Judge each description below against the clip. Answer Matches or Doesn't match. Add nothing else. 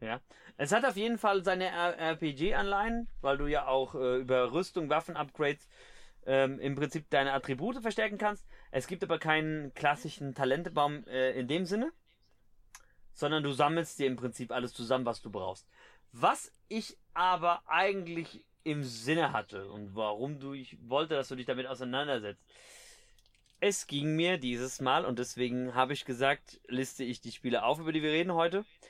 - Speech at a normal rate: Matches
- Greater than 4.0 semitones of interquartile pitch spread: Matches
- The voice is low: Doesn't match